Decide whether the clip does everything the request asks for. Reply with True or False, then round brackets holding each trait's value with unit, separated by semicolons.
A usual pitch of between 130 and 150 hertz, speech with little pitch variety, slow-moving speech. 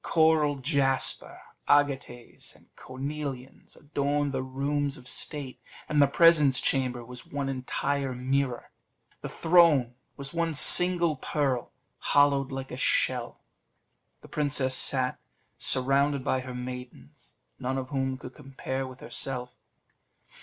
True (135 Hz; 1.9 semitones; 125 wpm)